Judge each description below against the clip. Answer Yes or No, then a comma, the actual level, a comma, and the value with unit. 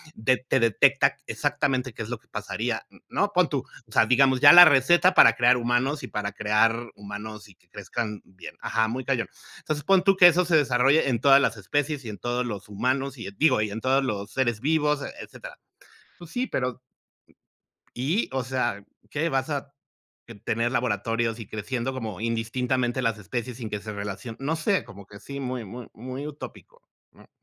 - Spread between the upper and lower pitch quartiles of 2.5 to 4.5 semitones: Yes, average, 3.9 semitones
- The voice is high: No, low, 125 Hz